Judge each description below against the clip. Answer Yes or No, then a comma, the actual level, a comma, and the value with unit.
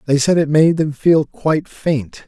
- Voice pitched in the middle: Yes, medium, 150 Hz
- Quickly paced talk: Yes, fast, 210 wpm